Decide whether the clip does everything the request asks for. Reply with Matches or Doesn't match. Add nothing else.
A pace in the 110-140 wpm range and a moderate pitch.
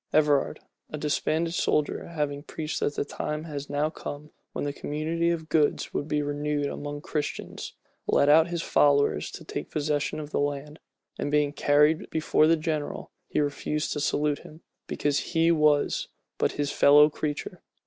Doesn't match